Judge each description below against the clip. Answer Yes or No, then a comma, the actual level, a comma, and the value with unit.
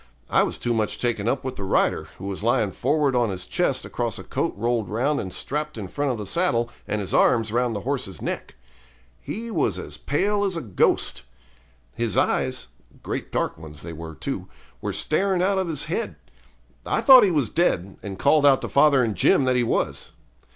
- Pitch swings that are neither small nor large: No, wide, 6.6 semitones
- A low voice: Yes, low, 120 Hz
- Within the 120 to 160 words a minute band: No, fast, 205 wpm